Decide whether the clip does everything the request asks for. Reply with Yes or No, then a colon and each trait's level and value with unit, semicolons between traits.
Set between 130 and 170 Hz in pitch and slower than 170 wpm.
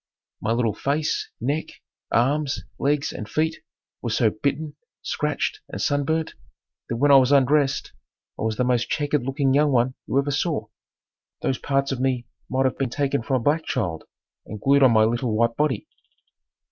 No: low, 135 Hz; average, 175 wpm